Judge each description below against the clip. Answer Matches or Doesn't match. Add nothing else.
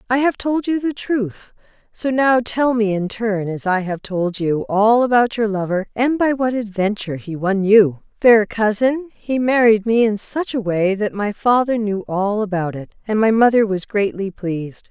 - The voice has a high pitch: Matches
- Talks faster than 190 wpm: Matches